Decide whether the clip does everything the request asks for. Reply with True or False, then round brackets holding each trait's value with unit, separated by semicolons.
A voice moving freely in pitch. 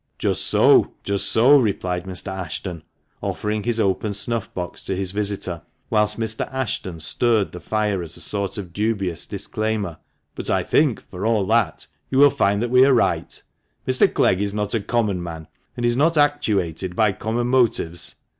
False (3.7 semitones)